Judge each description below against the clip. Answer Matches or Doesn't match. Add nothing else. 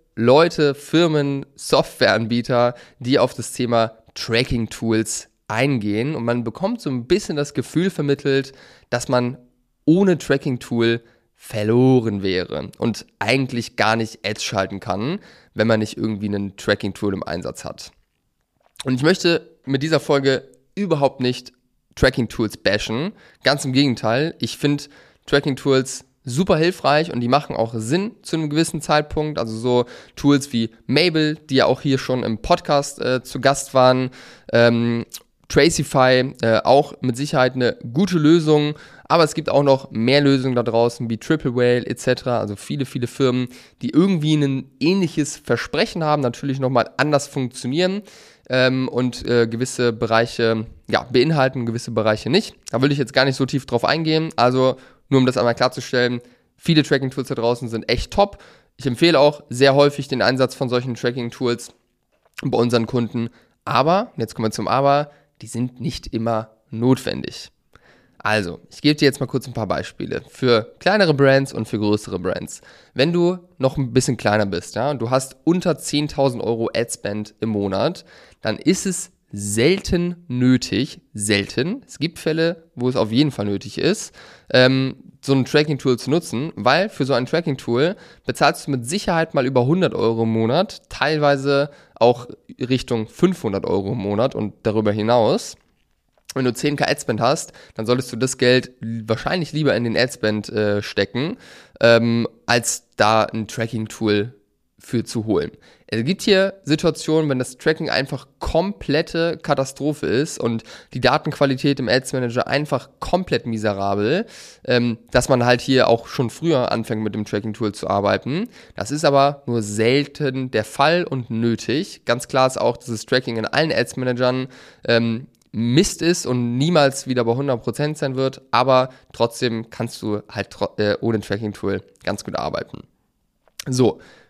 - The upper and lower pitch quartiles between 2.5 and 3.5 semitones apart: Doesn't match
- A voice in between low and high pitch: Doesn't match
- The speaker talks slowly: Doesn't match